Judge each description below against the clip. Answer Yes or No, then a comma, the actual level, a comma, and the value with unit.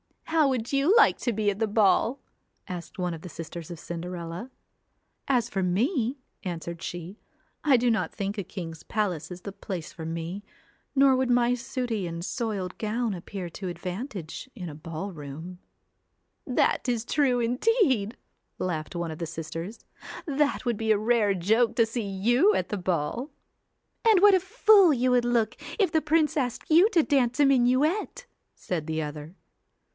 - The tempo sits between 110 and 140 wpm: No, average, 180 wpm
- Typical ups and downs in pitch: No, wide, 6.7 semitones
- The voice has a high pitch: Yes, high, 220 Hz